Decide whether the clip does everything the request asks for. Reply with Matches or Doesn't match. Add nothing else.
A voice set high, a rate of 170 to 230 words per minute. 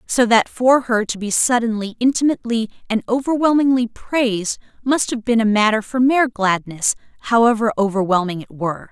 Doesn't match